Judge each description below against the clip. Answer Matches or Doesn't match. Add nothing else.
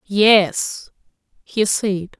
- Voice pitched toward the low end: Doesn't match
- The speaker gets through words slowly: Matches